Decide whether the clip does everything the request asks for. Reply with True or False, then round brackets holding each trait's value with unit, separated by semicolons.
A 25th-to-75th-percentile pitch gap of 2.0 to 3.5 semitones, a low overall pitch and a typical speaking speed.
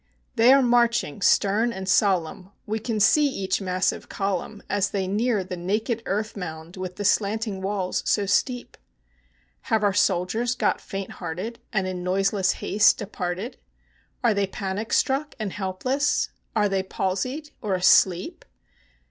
False (3.1 semitones; 200 Hz; 150 wpm)